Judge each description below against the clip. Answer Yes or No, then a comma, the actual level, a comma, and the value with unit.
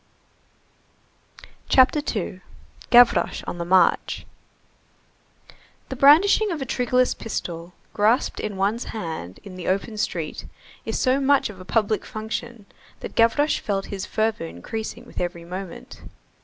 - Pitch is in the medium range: No, high, 215 Hz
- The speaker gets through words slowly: Yes, slow, 130 wpm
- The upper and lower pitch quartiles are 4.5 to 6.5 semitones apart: Yes, average, 5.2 semitones